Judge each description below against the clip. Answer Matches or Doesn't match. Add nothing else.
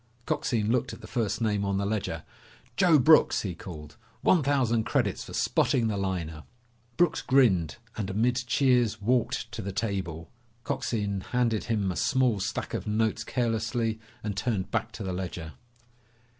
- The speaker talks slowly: Doesn't match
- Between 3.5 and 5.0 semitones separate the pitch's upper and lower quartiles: Matches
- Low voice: Matches